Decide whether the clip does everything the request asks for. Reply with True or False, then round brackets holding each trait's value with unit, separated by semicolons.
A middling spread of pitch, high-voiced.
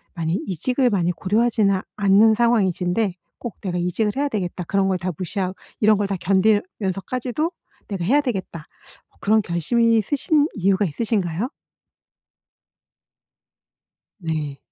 True (4.0 semitones; 200 Hz)